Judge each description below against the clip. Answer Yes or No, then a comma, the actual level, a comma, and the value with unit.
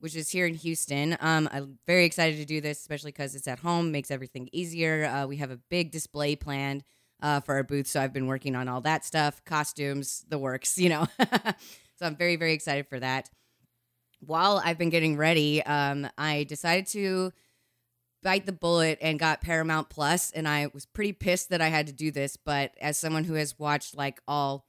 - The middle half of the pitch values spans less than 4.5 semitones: Yes, average, 2.8 semitones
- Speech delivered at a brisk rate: Yes, fast, 210 wpm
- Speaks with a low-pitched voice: No, medium, 150 Hz